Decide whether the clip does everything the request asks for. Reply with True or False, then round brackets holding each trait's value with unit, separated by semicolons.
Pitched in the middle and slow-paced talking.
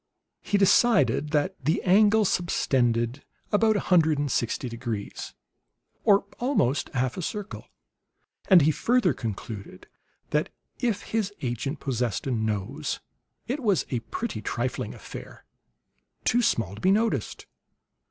True (155 Hz; 130 wpm)